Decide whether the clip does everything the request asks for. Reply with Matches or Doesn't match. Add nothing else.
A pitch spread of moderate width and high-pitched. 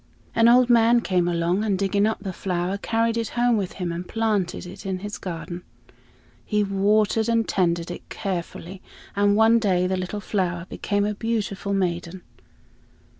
Matches